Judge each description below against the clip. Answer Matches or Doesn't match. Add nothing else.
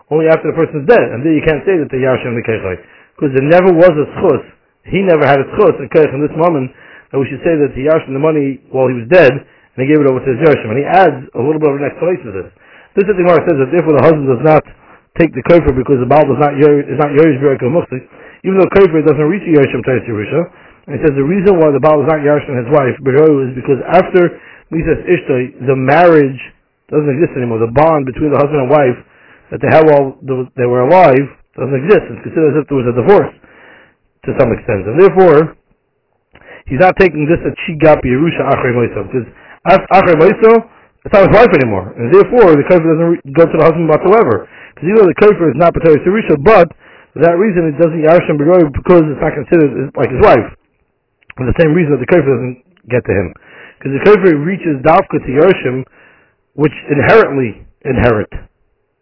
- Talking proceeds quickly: Matches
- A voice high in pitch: Doesn't match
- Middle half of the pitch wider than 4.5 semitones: Doesn't match